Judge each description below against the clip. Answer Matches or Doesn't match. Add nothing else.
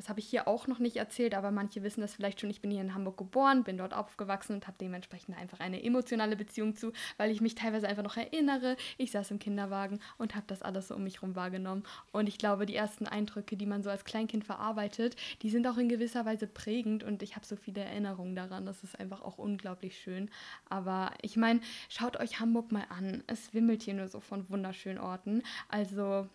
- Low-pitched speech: Doesn't match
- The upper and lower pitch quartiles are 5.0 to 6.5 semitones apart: Doesn't match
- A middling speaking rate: Doesn't match